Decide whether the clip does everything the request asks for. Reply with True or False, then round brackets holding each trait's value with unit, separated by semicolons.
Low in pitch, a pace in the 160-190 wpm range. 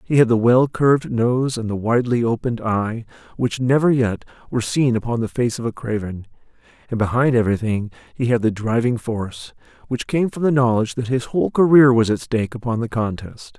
False (120 Hz; 200 wpm)